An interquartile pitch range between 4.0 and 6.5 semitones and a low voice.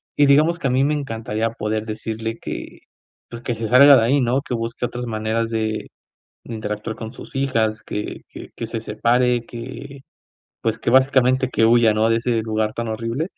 No: average, 2.7 semitones; low, 115 Hz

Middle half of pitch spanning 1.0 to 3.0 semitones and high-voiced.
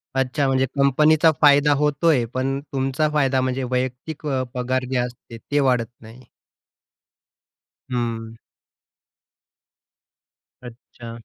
No: narrow, 2.5 semitones; low, 130 Hz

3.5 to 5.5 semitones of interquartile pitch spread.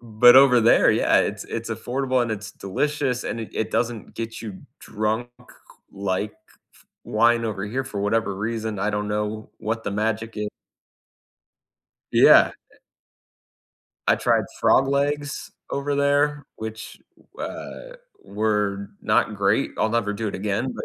No: average, 3.0 semitones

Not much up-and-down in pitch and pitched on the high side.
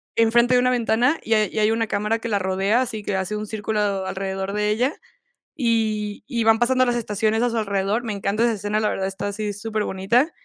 Yes: narrow, 2.3 semitones; high, 215 Hz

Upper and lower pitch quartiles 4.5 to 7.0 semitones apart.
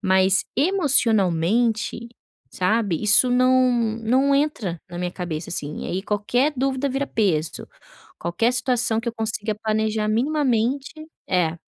Yes: average, 5.1 semitones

